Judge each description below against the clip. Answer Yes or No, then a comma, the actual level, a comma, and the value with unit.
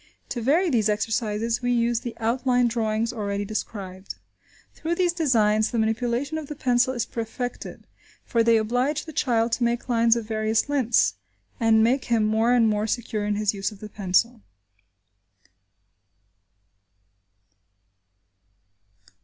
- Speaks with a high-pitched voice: Yes, high, 230 Hz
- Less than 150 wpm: Yes, average, 140 wpm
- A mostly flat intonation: Yes, narrow, 2.3 semitones